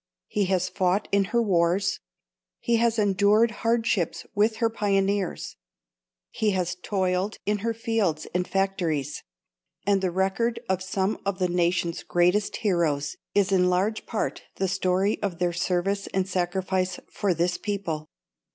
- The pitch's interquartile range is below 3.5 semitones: Yes, narrow, 2.4 semitones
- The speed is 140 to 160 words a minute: Yes, average, 145 wpm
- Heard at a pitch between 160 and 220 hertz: Yes, high, 190 Hz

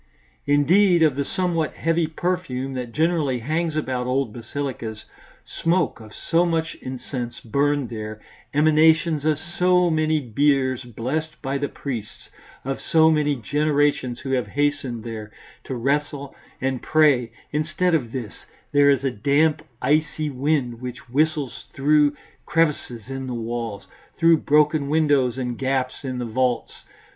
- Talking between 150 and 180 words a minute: No, average, 140 wpm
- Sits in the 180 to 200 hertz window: No, medium, 140 Hz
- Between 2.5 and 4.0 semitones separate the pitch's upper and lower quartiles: Yes, average, 3.7 semitones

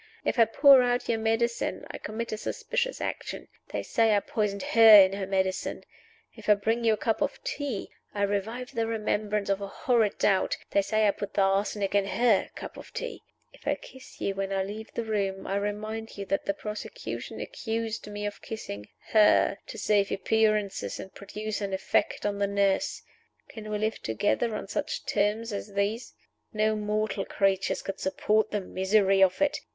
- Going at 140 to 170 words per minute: No, average, 190 wpm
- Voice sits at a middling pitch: No, high, 210 Hz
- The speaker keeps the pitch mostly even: Yes, narrow, 2.0 semitones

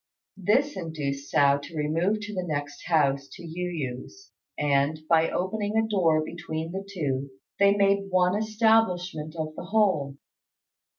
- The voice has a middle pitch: Yes, medium, 170 Hz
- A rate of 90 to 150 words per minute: Yes, average, 145 wpm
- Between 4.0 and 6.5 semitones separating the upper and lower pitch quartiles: Yes, average, 5.0 semitones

